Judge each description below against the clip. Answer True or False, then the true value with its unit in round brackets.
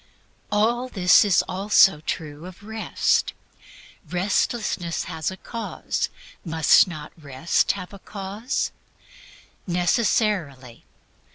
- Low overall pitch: False (185 Hz)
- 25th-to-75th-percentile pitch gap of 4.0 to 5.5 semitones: True (4.5 semitones)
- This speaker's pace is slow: True (95 wpm)